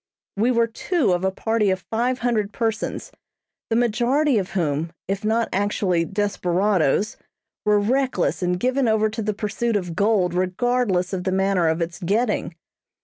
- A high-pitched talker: Yes, high, 205 Hz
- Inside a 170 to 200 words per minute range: No, average, 160 wpm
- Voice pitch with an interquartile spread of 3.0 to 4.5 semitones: Yes, average, 3.9 semitones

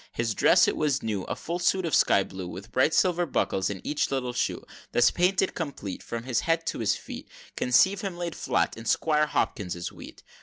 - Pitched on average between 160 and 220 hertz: No, low, 135 Hz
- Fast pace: Yes, fast, 215 wpm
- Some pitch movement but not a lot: No, wide, 7.5 semitones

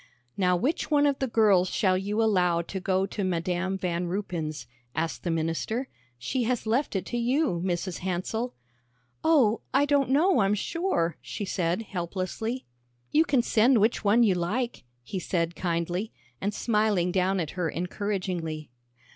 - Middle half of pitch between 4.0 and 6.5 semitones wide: Yes, average, 4.9 semitones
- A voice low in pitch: No, high, 195 Hz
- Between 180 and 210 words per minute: No, average, 160 wpm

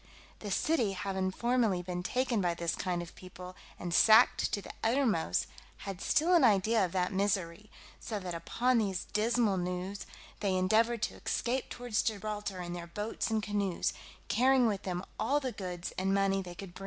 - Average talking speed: Yes, average, 180 wpm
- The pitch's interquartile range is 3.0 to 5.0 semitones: Yes, average, 3.7 semitones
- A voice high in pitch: Yes, high, 200 Hz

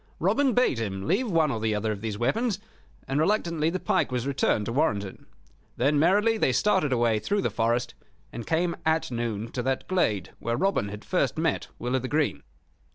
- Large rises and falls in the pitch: Yes, wide, 7.4 semitones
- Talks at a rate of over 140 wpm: Yes, average, 200 wpm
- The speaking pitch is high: No, low, 135 Hz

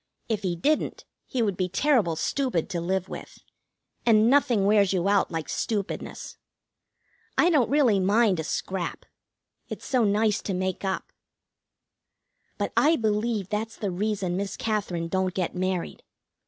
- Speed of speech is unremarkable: Yes, average, 150 wpm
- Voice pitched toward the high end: Yes, high, 200 Hz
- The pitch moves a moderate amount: Yes, average, 3.4 semitones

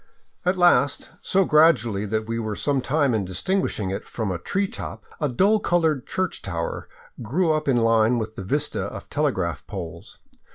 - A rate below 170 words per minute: No, average, 175 wpm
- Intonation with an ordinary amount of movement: No, wide, 6.9 semitones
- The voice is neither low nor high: No, low, 125 Hz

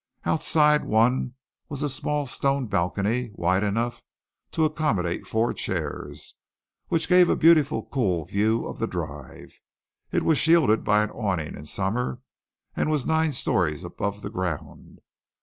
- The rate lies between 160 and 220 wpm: No, average, 145 wpm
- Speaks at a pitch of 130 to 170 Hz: No, low, 115 Hz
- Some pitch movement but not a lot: No, wide, 7.0 semitones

